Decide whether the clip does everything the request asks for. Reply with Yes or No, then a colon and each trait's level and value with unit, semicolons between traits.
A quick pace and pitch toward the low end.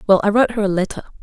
No: fast, 295 wpm; high, 205 Hz